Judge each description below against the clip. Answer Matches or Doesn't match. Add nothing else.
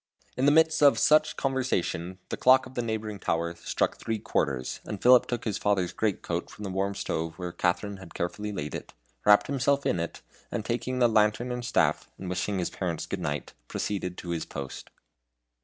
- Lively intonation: Matches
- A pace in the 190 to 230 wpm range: Matches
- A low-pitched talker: Matches